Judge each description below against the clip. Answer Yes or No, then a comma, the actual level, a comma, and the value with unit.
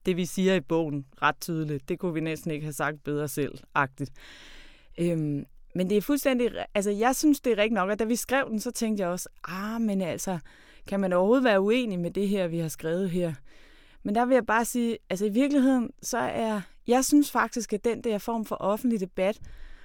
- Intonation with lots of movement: Yes, wide, 5.7 semitones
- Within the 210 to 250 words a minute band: Yes, average, 220 wpm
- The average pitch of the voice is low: No, high, 195 Hz